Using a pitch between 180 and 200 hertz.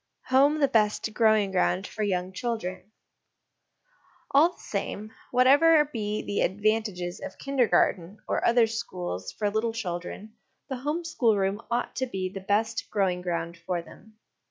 No: high, 215 Hz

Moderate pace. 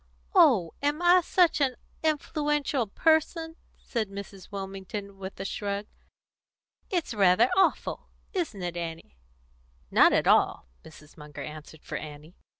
No: slow, 130 wpm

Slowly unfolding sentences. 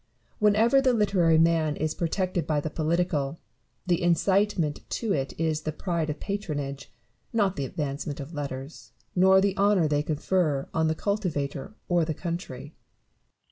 No: average, 150 wpm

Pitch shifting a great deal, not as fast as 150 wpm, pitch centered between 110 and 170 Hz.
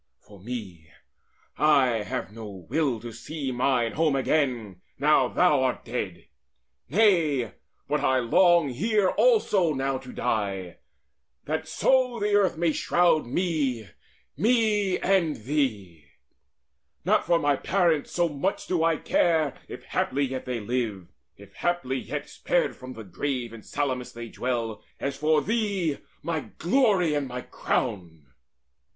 Yes: wide, 6.6 semitones; average, 140 wpm; medium, 140 Hz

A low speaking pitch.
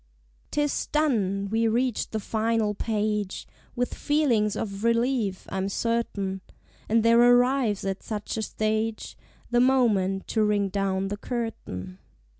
No: high, 220 Hz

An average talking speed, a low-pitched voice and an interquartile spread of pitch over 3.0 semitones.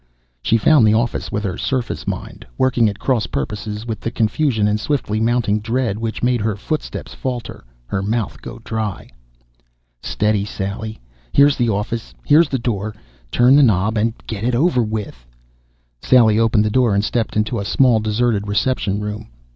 No: average, 170 wpm; low, 110 Hz; narrow, 2.6 semitones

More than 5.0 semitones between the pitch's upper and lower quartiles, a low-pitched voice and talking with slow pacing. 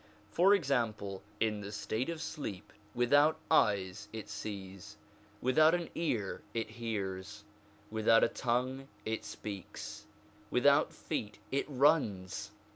Yes: wide, 5.5 semitones; low, 115 Hz; slow, 120 wpm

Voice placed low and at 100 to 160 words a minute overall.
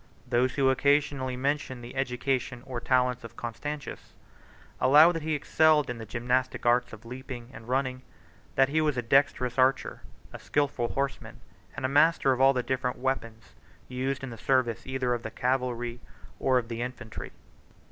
No: low, 130 Hz; average, 170 wpm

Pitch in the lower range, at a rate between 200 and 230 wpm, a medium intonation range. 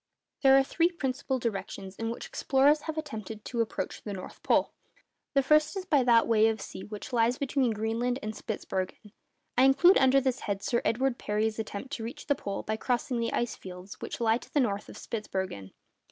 No: high, 235 Hz; fast, 205 wpm; average, 4.0 semitones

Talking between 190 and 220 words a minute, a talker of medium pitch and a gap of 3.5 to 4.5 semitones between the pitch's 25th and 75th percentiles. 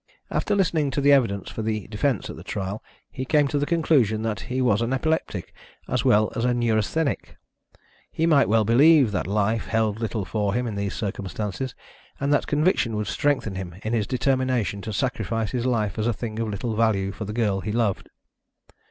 No: average, 200 wpm; low, 115 Hz; average, 4.0 semitones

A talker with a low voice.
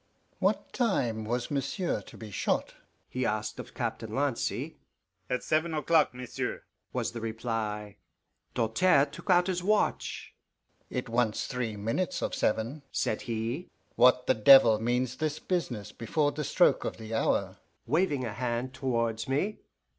Yes: low, 125 Hz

